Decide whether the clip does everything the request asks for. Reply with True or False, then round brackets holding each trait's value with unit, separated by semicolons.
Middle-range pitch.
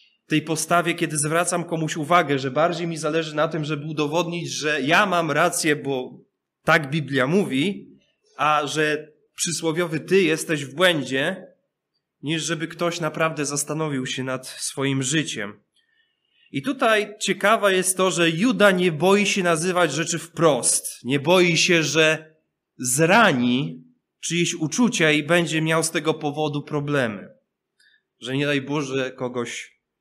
True (160 Hz)